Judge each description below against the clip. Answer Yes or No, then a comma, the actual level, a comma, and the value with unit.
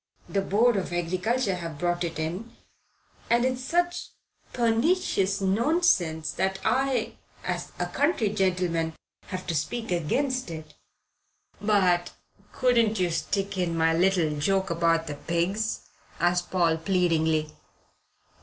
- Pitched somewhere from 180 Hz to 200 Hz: Yes, medium, 185 Hz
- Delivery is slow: Yes, slow, 125 wpm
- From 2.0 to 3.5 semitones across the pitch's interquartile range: No, average, 5.2 semitones